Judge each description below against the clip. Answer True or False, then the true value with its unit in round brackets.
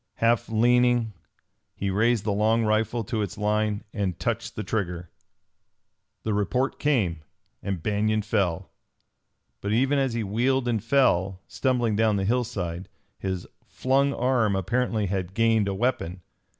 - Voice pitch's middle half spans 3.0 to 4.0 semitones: True (3.5 semitones)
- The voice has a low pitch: True (110 Hz)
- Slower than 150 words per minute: True (140 wpm)